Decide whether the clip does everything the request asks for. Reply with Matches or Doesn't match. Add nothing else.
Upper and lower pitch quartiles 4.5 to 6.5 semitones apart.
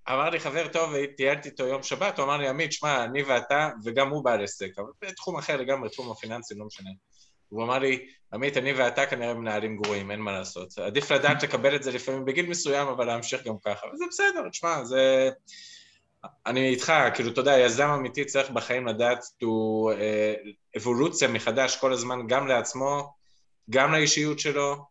Doesn't match